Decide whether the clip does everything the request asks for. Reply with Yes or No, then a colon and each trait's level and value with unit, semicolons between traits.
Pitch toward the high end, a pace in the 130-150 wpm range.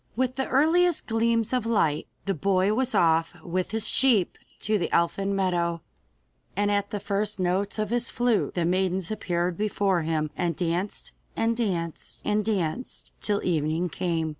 No: high, 195 Hz; average, 165 wpm